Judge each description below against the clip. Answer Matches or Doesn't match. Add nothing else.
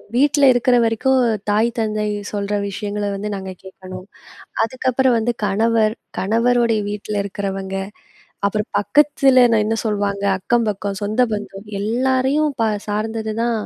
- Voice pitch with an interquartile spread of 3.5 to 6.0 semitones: Doesn't match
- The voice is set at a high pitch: Matches